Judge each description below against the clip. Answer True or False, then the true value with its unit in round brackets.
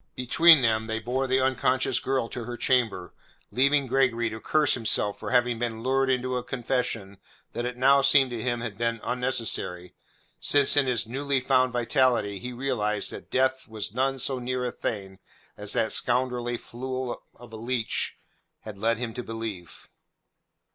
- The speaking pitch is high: False (125 Hz)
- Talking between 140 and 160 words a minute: False (170 wpm)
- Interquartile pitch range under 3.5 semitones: True (2.5 semitones)